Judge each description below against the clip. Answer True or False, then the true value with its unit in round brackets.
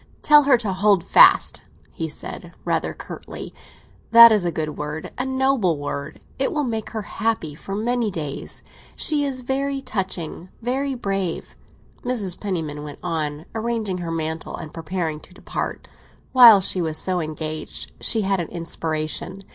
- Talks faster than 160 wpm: False (155 wpm)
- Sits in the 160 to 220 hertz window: True (190 Hz)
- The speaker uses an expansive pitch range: True (6.7 semitones)